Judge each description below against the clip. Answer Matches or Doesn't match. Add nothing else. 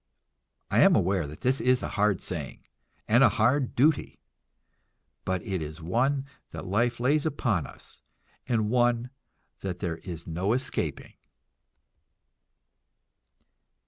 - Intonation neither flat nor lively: Doesn't match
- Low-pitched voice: Matches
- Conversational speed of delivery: Doesn't match